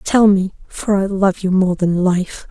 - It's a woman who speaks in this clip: Yes, female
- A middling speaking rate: No, fast, 215 wpm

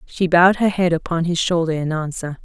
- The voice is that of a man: No, female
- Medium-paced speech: No, fast, 220 wpm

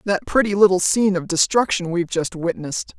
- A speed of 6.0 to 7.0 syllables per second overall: Yes, 6.1 syllables/s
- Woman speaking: Yes, female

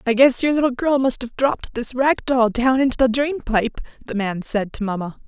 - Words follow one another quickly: Yes, fast, 240 wpm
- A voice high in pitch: Yes, high, 245 Hz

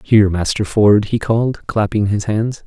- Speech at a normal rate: Yes, average, 180 wpm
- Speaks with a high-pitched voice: No, low, 105 Hz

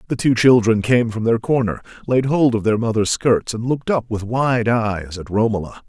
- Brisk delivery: Yes, fast, 215 wpm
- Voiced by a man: Yes, male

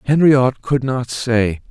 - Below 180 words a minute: Yes, average, 140 wpm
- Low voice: Yes, low, 125 Hz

